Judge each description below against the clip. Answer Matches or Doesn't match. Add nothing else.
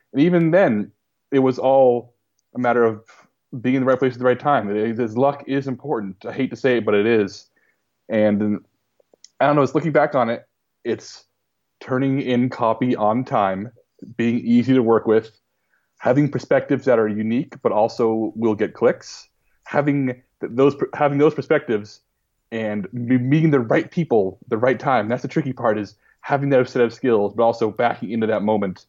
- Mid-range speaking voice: Doesn't match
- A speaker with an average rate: Matches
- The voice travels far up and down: Doesn't match